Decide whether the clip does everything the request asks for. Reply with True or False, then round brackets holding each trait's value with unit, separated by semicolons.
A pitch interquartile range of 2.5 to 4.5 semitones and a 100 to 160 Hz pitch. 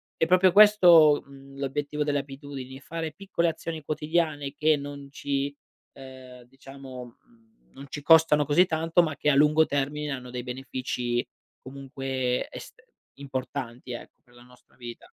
True (2.9 semitones; 140 Hz)